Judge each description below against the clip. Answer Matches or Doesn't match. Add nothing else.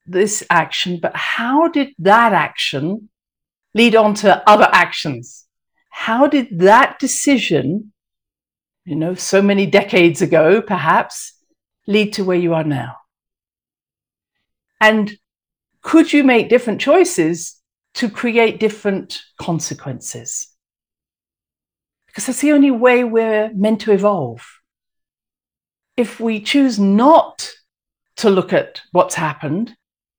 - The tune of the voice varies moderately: Doesn't match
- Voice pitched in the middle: Doesn't match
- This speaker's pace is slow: Matches